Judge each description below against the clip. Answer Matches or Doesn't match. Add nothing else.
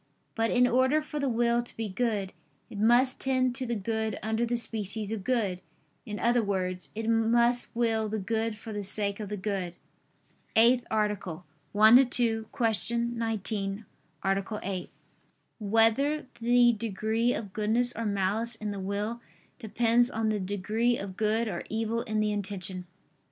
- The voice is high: Matches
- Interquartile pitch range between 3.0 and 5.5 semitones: Doesn't match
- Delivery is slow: Doesn't match